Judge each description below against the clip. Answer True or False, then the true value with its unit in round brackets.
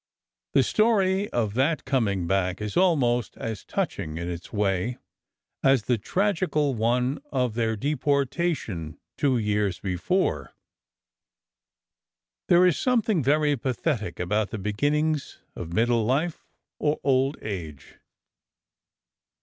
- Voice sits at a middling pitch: False (125 Hz)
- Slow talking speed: True (115 wpm)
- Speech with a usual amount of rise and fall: False (6.6 semitones)